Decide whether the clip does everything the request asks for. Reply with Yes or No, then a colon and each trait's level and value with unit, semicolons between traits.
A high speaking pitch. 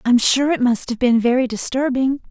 Yes: very high, 250 Hz